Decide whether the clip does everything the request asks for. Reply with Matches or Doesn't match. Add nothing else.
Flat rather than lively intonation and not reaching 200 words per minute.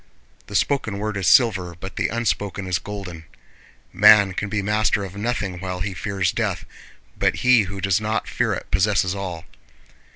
Matches